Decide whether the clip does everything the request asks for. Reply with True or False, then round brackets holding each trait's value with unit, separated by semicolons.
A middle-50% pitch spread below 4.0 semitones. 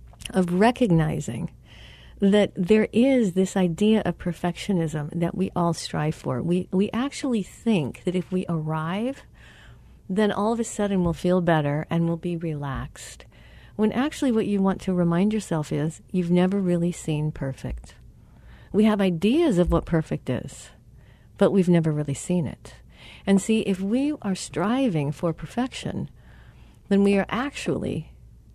False (4.3 semitones)